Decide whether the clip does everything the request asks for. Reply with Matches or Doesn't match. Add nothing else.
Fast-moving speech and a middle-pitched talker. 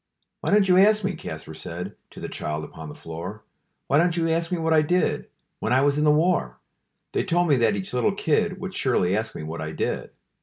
Matches